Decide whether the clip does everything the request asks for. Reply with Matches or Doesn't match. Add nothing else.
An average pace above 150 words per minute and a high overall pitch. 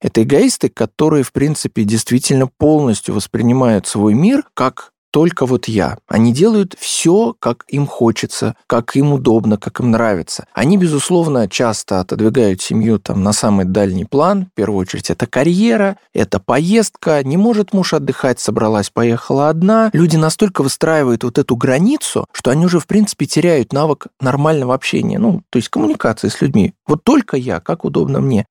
Doesn't match